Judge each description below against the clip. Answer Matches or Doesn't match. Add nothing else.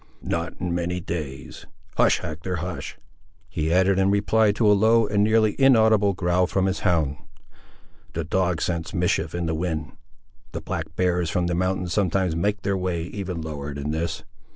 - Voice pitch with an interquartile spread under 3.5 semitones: Matches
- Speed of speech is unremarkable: Matches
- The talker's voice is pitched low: Matches